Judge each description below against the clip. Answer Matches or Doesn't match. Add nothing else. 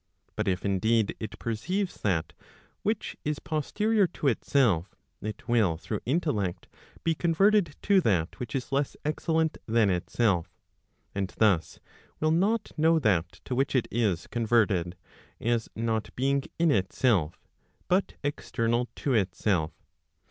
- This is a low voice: Matches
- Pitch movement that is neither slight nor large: Doesn't match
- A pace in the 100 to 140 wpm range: Matches